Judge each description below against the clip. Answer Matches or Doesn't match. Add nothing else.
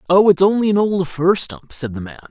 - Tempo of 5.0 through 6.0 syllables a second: Matches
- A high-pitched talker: Doesn't match